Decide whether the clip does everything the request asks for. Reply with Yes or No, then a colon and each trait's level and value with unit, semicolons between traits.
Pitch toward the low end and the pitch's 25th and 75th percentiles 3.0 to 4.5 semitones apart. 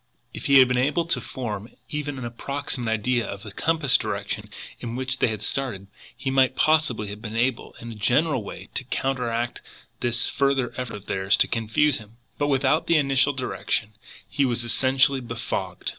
Yes: low, 125 Hz; average, 3.3 semitones